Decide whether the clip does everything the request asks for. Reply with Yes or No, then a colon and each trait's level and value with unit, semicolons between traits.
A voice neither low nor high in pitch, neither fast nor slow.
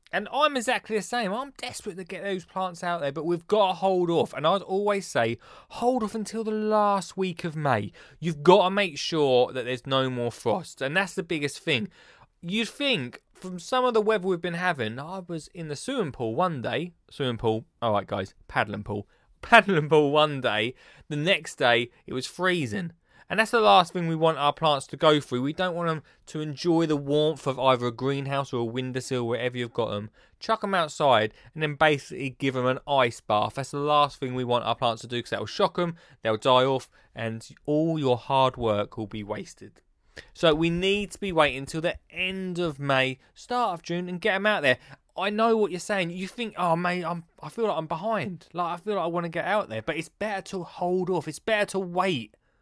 No: medium, 165 Hz; fast, 230 wpm